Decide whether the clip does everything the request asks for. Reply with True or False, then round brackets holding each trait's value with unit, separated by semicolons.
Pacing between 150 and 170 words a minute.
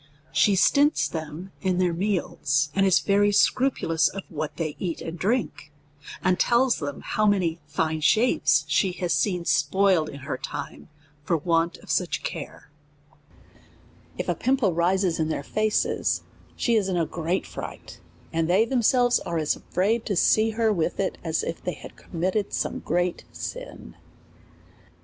True (165 wpm)